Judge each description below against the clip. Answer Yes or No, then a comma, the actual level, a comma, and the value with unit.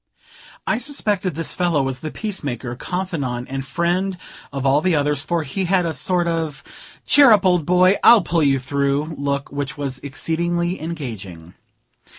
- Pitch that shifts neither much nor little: Yes, average, 4.6 semitones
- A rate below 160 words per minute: No, average, 165 wpm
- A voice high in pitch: No, medium, 160 Hz